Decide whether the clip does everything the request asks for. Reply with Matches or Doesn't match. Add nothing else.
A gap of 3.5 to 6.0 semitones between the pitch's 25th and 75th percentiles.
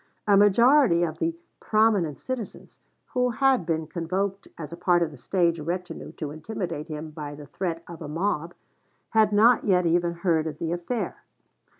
Matches